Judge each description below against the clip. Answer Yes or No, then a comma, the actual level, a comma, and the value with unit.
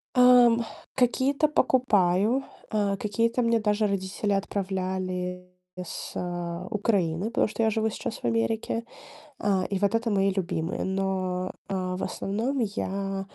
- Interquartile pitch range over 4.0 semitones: No, average, 3.6 semitones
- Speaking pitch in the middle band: No, high, 200 Hz